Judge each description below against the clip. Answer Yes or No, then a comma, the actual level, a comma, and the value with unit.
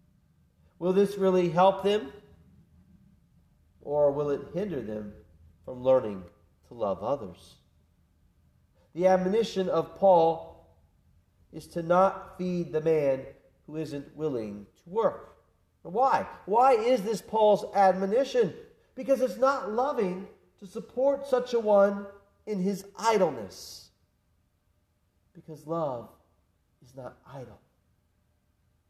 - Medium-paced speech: No, slow, 110 wpm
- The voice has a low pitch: No, medium, 170 Hz